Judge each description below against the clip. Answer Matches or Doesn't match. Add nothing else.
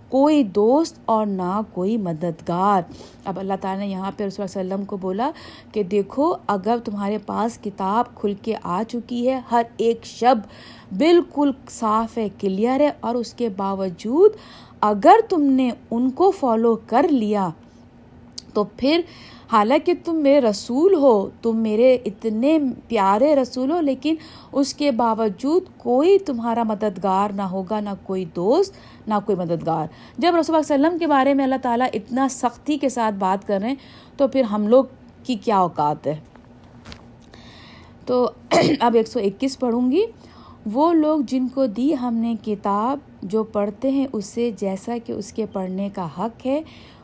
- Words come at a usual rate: Matches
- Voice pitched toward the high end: Matches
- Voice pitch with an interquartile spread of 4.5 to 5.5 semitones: Matches